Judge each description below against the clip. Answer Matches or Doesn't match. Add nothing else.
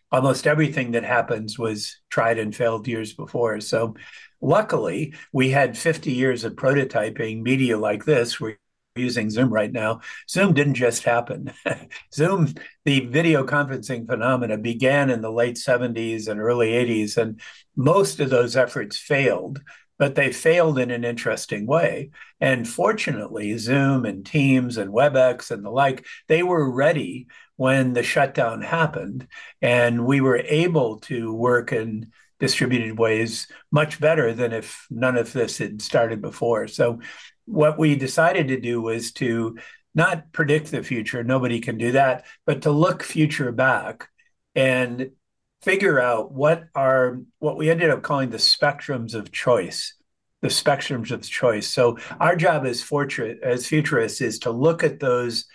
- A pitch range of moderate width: Matches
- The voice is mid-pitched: Doesn't match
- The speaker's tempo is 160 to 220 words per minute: Doesn't match